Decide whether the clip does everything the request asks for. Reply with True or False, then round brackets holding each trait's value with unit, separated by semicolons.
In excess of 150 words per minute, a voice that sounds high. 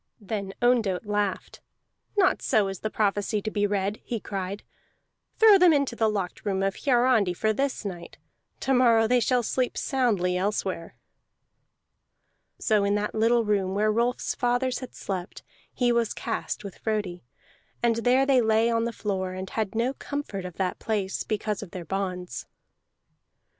True (165 wpm; 215 Hz)